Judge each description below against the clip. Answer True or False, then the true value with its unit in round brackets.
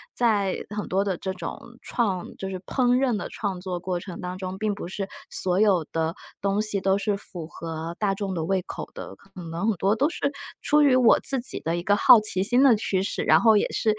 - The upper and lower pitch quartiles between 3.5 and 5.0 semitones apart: False (2.9 semitones)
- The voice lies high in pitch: True (195 Hz)